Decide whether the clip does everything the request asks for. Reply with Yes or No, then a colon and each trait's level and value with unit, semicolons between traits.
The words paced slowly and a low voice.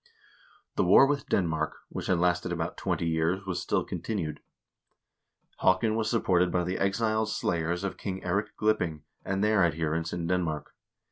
No: average, 155 wpm; very low, 90 Hz